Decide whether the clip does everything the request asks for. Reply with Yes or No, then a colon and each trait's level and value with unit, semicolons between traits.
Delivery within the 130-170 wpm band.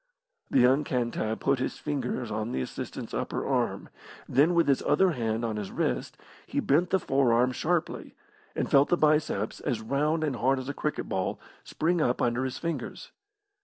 No: average, 180 wpm